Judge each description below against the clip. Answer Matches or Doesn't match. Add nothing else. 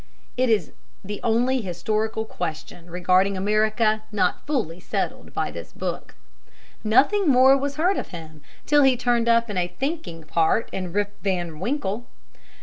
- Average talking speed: Matches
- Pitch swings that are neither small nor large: Doesn't match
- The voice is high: Matches